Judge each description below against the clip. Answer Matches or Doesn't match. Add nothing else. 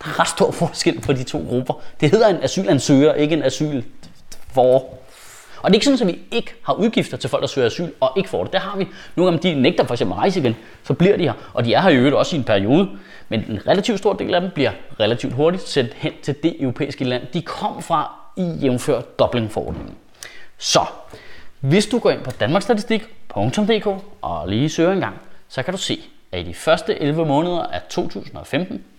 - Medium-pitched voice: Matches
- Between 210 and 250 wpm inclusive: Matches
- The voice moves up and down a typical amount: Doesn't match